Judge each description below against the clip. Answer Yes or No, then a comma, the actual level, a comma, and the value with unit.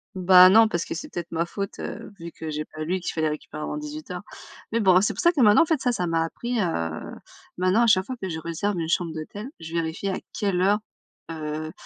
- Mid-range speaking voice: Yes, medium, 180 Hz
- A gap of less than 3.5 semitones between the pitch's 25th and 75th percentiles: No, average, 4.5 semitones